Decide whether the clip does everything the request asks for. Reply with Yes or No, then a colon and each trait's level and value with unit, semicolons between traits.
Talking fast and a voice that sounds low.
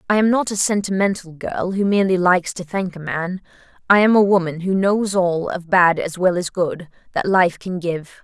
No: fast, 220 wpm; medium, 185 Hz